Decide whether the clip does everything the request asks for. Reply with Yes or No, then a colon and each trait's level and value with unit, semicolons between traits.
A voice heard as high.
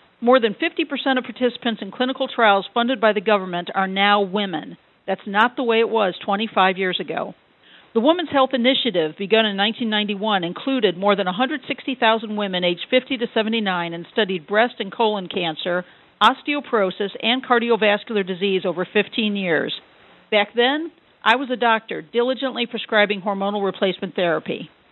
Yes: high, 220 Hz